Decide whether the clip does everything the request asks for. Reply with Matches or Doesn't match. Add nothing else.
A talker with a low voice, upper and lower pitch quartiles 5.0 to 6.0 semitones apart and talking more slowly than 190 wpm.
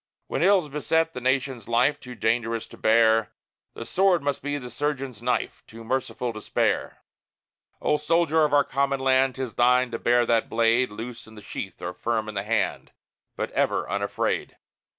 Doesn't match